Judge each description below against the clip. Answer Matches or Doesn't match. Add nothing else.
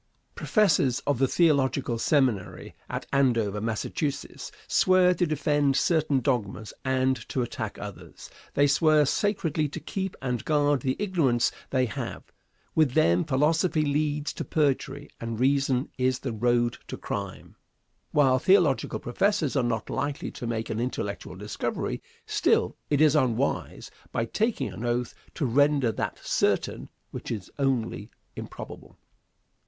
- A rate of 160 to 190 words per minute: Doesn't match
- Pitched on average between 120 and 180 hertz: Matches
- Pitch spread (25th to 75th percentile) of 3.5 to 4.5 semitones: Matches